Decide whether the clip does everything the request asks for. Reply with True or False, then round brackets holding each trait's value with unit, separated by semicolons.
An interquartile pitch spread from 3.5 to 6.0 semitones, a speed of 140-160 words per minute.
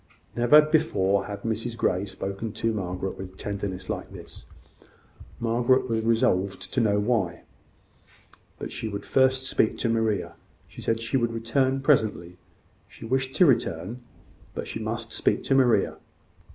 True (3.8 semitones; 150 wpm)